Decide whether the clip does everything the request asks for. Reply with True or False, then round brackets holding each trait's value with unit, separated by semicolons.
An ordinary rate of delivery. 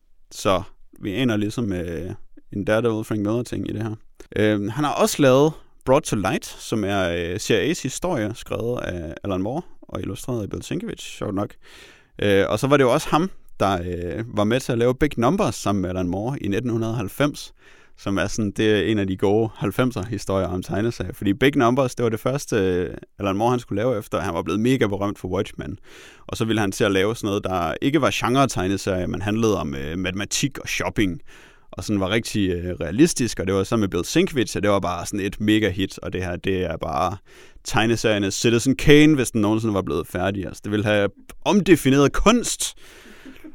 True (215 wpm)